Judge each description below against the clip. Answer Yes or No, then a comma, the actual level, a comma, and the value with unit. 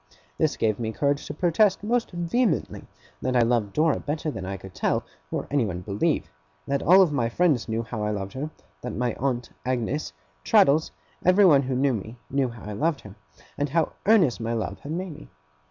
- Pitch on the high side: No, low, 135 Hz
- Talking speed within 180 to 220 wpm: Yes, average, 195 wpm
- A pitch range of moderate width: No, wide, 6.0 semitones